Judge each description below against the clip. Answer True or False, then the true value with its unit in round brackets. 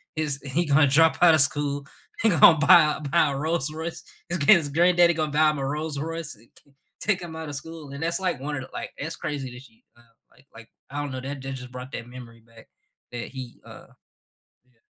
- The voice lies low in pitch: False (145 Hz)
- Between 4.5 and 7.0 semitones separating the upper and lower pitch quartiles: False (3.4 semitones)